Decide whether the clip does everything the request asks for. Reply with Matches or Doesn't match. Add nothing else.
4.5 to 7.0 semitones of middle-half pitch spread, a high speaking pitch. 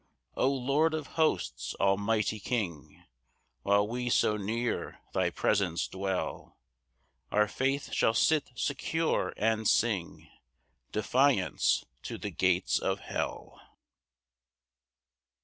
Doesn't match